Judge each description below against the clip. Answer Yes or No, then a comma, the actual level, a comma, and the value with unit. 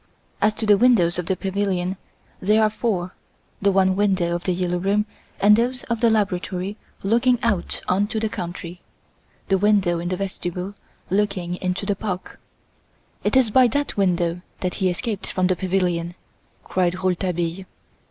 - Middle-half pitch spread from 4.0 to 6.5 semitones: No, average, 2.8 semitones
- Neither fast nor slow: Yes, average, 165 wpm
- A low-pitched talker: No, high, 190 Hz